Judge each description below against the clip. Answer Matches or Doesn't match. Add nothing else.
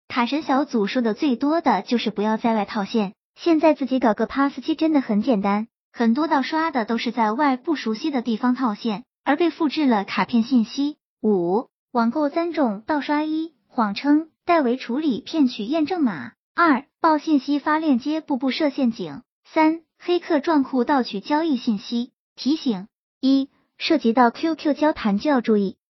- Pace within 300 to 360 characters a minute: Doesn't match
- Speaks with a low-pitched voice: Doesn't match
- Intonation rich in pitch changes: Doesn't match